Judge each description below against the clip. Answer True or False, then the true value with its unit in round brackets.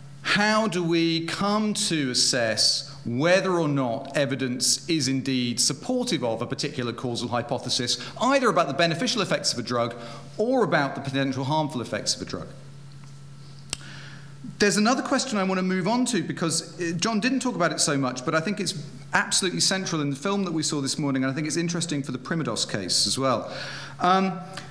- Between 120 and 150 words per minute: False (190 wpm)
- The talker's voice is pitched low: False (155 Hz)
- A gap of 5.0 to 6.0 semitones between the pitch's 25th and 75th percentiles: True (5.5 semitones)